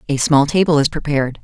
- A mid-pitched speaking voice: Yes, medium, 145 Hz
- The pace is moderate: No, fast, 210 wpm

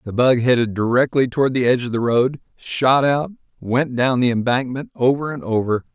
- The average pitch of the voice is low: Yes, low, 125 Hz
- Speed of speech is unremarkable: Yes, average, 190 wpm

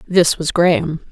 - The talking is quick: No, average, 160 wpm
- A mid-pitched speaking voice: Yes, medium, 170 Hz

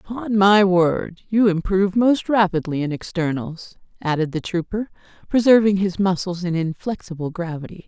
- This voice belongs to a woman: Yes, female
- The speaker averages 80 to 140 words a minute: Yes, slow, 135 wpm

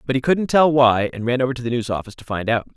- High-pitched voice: No, low, 125 Hz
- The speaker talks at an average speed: No, fast, 325 wpm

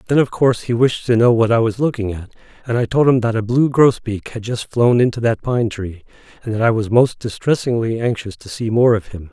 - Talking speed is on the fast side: Yes, fast, 250 wpm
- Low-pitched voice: Yes, low, 115 Hz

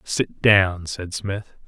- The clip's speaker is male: Yes, male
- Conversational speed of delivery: Yes, average, 145 wpm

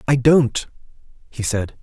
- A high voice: No, low, 125 Hz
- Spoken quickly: No, slow, 130 wpm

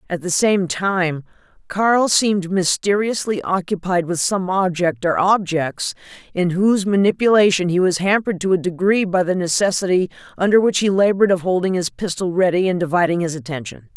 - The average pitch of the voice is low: No, medium, 185 Hz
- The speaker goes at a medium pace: Yes, average, 165 wpm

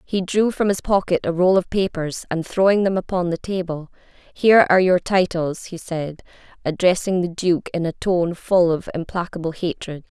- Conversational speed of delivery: Yes, average, 180 wpm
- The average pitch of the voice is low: No, medium, 175 Hz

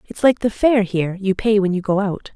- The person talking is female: Yes, female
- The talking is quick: Yes, fast, 280 wpm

